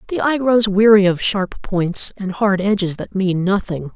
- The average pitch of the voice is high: Yes, high, 200 Hz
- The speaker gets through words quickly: No, average, 195 wpm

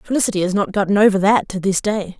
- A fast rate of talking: Yes, fast, 245 wpm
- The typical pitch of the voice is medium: No, high, 200 Hz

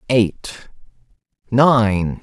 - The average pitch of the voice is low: Yes, low, 110 Hz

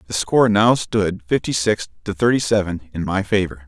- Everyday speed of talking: Yes, average, 195 wpm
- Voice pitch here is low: Yes, low, 100 Hz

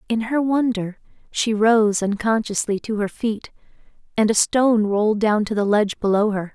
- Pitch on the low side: No, high, 215 Hz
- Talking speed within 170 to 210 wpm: Yes, average, 175 wpm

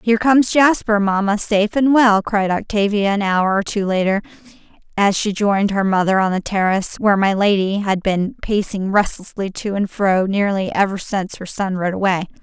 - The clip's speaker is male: No, female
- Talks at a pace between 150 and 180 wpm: No, average, 190 wpm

